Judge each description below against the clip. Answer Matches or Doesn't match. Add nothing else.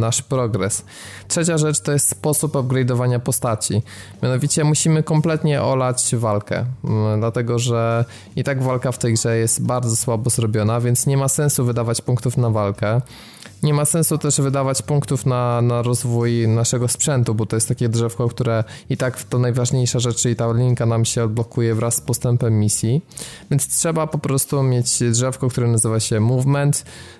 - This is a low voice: Matches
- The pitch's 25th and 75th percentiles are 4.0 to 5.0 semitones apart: Doesn't match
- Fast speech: Matches